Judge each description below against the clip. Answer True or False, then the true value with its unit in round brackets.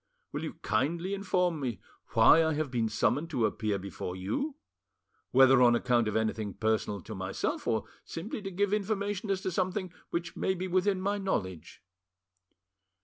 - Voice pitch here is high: False (160 Hz)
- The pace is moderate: True (165 wpm)